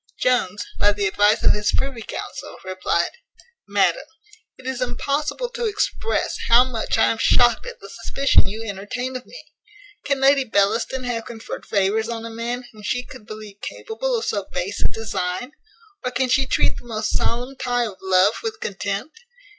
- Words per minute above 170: Yes, average, 180 wpm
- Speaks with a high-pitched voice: Yes, high, 235 Hz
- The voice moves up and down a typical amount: Yes, average, 4.0 semitones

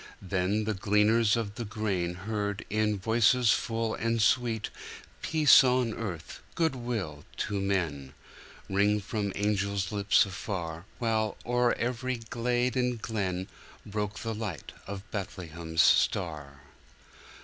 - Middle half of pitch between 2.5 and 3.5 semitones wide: Yes, average, 3.2 semitones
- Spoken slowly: Yes, slow, 115 wpm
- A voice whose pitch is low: Yes, low, 105 Hz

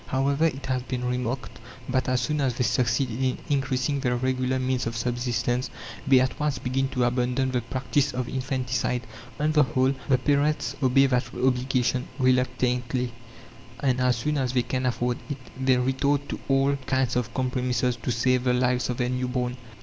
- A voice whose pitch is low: Yes, low, 130 Hz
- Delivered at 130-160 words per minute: No, average, 180 wpm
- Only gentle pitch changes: Yes, narrow, 1.2 semitones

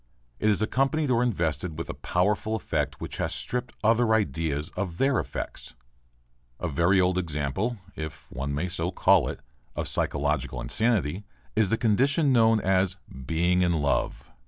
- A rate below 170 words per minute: Yes, average, 160 wpm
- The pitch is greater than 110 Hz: No, very low, 95 Hz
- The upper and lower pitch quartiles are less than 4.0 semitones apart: No, wide, 5.6 semitones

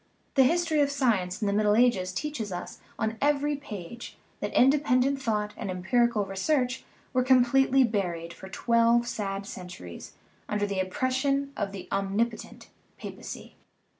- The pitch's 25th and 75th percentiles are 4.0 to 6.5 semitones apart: Yes, average, 5.2 semitones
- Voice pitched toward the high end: Yes, high, 230 Hz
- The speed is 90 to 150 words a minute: Yes, average, 145 wpm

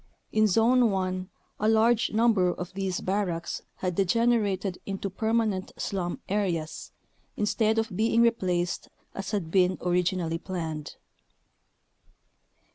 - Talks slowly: Yes, slow, 115 wpm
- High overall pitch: Yes, high, 195 Hz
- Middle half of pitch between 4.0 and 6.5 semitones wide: No, average, 3.4 semitones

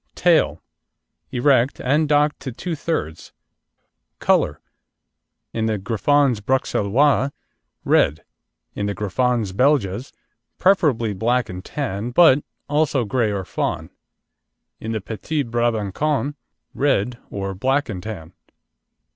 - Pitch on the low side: Yes, low, 120 Hz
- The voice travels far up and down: Yes, wide, 5.8 semitones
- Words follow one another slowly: Yes, slow, 110 wpm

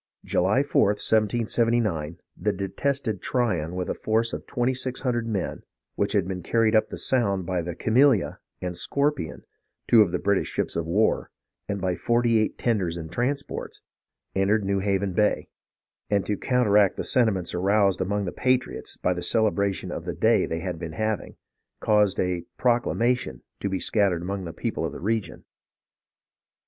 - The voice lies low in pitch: Yes, low, 100 Hz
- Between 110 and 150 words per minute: No, average, 170 wpm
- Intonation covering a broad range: No, average, 4.1 semitones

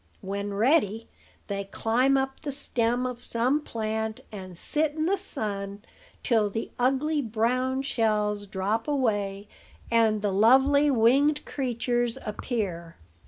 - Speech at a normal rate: No, slow, 125 wpm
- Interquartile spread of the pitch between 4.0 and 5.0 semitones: Yes, average, 4.3 semitones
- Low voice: No, high, 230 Hz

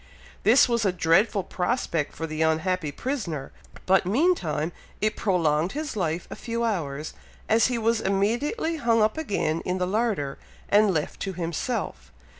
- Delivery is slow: No, average, 155 wpm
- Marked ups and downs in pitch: Yes, wide, 6.1 semitones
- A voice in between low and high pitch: No, high, 195 Hz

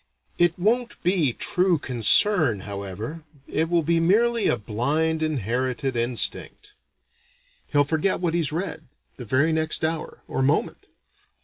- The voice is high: No, medium, 160 Hz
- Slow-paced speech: Yes, slow, 130 wpm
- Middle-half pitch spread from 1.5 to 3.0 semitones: No, average, 5.3 semitones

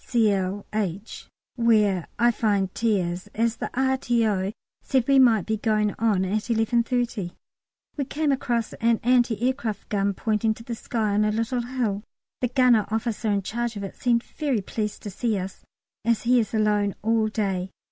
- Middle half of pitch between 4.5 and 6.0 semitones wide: No, average, 2.7 semitones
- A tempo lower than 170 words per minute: No, average, 175 wpm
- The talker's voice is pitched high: Yes, high, 220 Hz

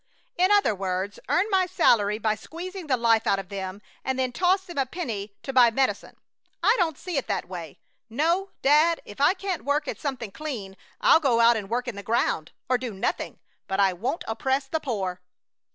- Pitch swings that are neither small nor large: No, wide, 7.7 semitones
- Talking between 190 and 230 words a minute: Yes, fast, 205 wpm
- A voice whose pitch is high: Yes, very high, 255 Hz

